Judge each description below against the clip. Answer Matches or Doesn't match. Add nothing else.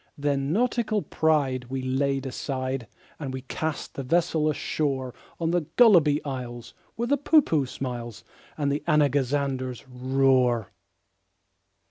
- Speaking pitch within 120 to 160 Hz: Matches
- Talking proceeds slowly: Matches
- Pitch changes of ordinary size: Matches